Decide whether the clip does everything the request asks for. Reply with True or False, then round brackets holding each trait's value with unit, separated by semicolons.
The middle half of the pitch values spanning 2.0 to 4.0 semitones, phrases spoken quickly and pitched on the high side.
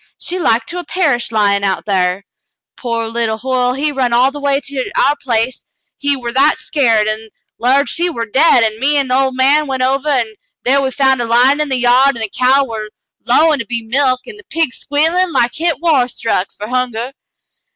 True (3.5 semitones; 215 wpm; 255 Hz)